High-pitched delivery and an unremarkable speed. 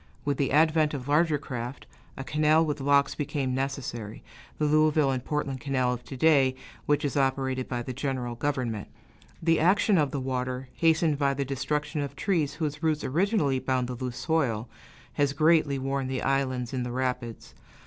No: medium, 140 Hz; average, 180 wpm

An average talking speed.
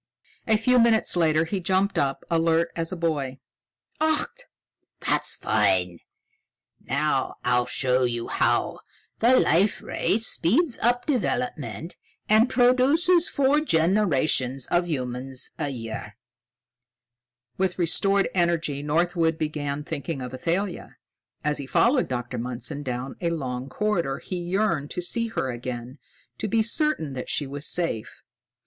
No: slow, 130 wpm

